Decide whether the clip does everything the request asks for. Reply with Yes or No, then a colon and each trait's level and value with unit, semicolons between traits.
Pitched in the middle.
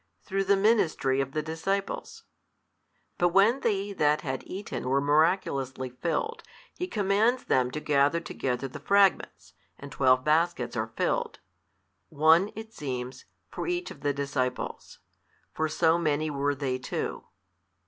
Yes: medium, 155 Hz